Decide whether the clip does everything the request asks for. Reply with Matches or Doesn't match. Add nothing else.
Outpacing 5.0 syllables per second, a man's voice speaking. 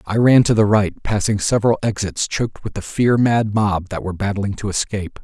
Matches